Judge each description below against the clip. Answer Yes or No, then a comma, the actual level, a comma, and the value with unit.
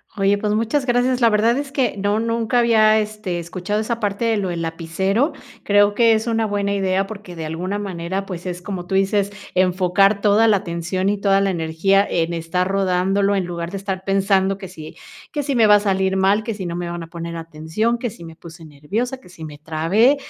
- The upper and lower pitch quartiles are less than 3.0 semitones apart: No, average, 3.5 semitones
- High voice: Yes, high, 195 Hz